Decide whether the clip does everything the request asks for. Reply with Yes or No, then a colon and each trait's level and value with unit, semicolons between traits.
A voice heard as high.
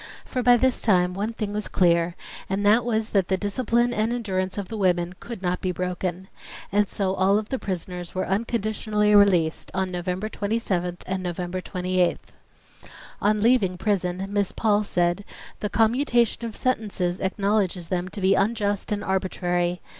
Yes: high, 195 Hz